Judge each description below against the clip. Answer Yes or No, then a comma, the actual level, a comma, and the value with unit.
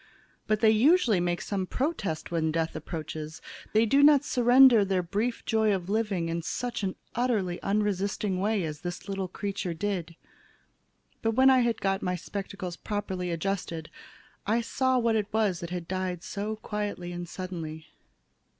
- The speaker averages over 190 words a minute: No, average, 160 wpm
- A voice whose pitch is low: No, high, 195 Hz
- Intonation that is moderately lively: Yes, average, 3.9 semitones